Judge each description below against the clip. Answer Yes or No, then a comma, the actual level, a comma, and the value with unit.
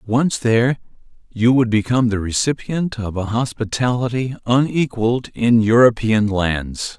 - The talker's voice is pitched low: Yes, low, 115 Hz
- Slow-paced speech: Yes, slow, 120 wpm